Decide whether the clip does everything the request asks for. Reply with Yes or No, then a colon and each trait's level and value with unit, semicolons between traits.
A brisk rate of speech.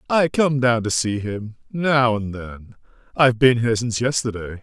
No: average, 170 wpm